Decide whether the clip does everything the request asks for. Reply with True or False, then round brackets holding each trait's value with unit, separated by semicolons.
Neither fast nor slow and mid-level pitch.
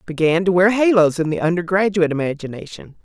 True (160 wpm; 175 Hz)